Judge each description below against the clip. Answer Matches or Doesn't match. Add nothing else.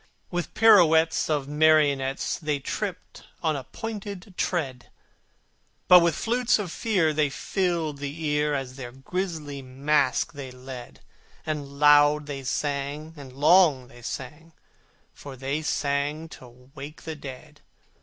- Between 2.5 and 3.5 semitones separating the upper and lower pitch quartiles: Matches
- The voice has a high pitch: Doesn't match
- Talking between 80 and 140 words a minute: Matches